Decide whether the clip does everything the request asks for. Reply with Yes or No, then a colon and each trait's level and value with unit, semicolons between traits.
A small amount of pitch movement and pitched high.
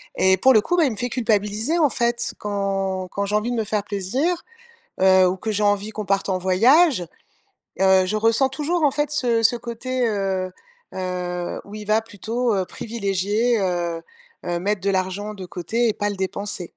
No: average, 3.8 semitones; high, 205 Hz